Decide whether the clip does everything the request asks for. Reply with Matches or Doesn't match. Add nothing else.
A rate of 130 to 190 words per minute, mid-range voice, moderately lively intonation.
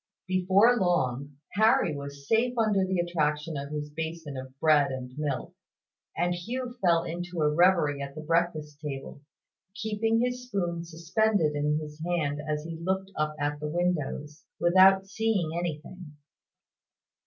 Matches